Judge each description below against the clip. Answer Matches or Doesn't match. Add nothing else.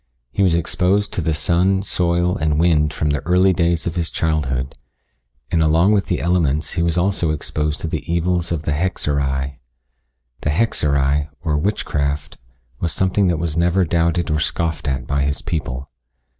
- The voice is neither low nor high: Doesn't match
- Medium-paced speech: Matches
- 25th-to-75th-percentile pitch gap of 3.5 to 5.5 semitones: Doesn't match